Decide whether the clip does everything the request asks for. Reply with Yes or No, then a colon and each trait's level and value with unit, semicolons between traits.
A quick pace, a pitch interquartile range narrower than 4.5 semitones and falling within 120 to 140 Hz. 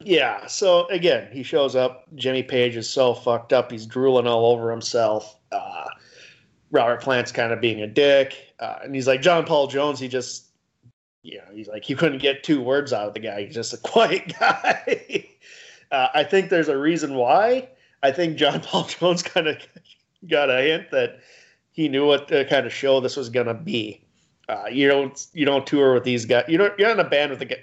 No: fast, 215 wpm; average, 5.0 semitones; low, 135 Hz